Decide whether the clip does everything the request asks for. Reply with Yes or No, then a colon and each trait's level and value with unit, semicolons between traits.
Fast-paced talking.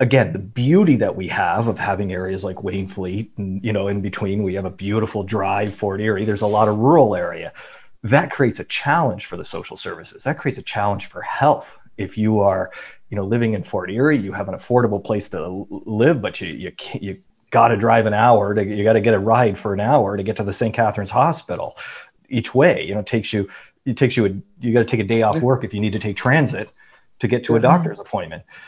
Yes: fast, 240 wpm